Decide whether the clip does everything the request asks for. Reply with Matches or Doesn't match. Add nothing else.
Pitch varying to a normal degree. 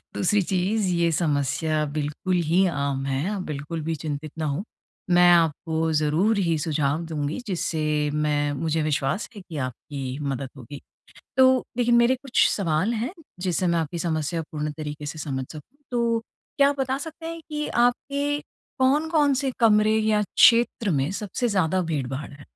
Doesn't match